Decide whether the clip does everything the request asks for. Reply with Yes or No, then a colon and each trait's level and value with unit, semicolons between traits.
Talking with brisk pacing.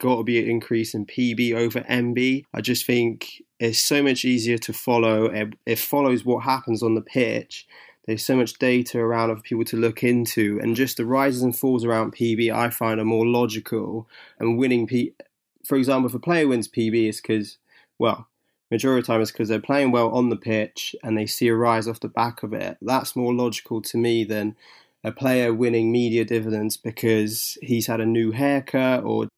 Yes: fast, 210 wpm